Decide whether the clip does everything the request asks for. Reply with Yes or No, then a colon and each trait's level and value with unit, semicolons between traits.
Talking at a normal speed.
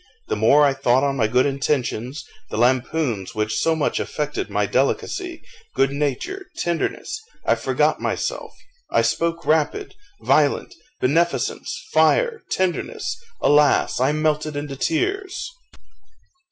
No: slow, 125 wpm